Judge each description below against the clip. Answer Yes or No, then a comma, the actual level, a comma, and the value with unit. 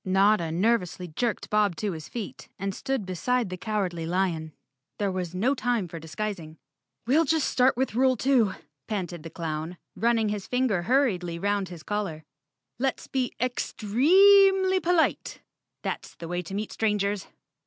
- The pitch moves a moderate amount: No, wide, 5.8 semitones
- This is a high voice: Yes, high, 205 Hz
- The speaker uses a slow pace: No, average, 155 wpm